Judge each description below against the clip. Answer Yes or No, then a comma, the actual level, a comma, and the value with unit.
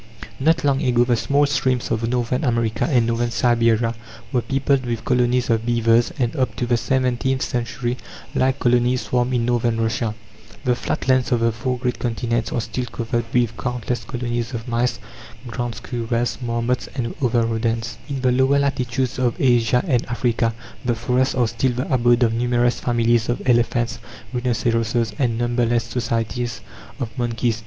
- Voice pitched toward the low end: Yes, low, 120 Hz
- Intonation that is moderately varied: No, narrow, 1.3 semitones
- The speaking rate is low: No, average, 165 wpm